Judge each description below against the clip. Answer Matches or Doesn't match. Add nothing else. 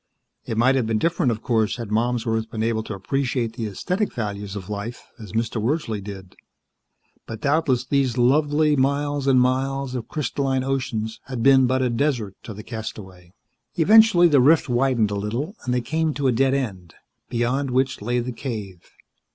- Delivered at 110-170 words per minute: Doesn't match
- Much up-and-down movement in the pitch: Doesn't match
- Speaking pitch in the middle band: Doesn't match